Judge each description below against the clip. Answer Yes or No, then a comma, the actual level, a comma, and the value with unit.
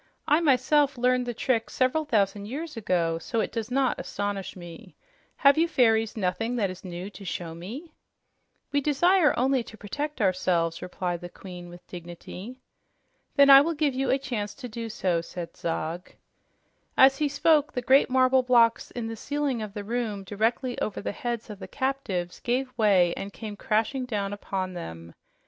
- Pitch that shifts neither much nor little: No, wide, 6.0 semitones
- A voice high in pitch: Yes, high, 225 Hz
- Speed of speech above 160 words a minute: Yes, average, 180 wpm